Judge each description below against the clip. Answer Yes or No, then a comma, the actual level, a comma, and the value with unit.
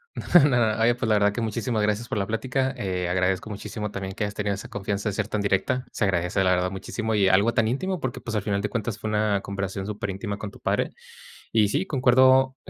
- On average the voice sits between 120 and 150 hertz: No, low, 105 Hz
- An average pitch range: Yes, average, 3.0 semitones